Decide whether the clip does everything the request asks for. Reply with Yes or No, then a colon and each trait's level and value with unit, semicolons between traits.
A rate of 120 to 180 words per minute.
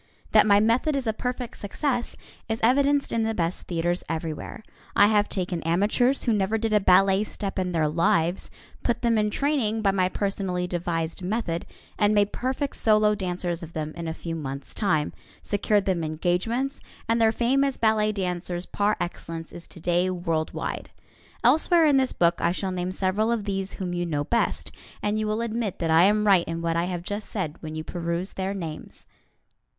No: average, 195 wpm